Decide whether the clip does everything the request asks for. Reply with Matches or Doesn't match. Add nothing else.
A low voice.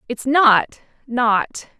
Doesn't match